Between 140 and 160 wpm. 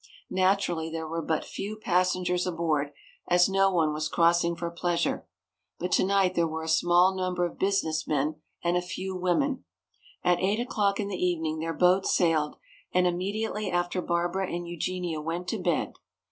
No: average, 170 wpm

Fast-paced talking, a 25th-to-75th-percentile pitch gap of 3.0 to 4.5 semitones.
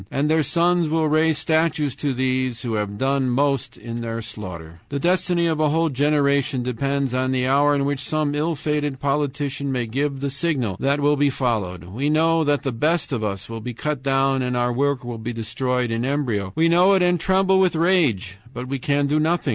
Yes: fast, 215 wpm; average, 3.7 semitones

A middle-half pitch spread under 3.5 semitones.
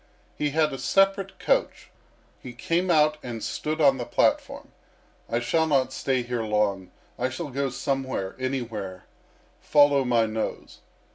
No: average, 4.3 semitones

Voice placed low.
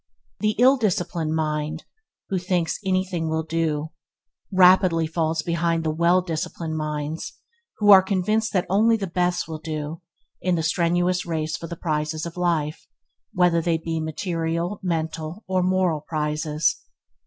No: medium, 165 Hz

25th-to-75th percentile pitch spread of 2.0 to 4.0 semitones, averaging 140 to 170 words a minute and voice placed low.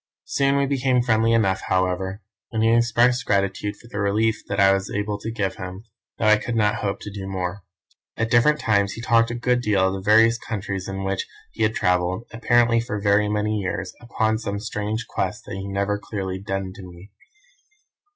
No: average, 2.8 semitones; average, 200 wpm; low, 105 Hz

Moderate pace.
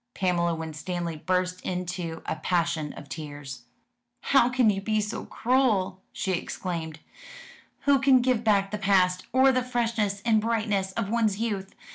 Yes: average, 150 wpm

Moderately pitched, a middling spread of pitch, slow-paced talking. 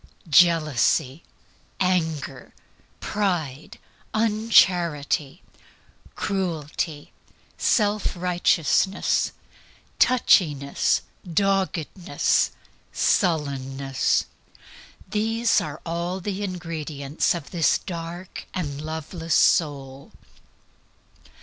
Yes: medium, 165 Hz; average, 4.4 semitones; slow, 55 wpm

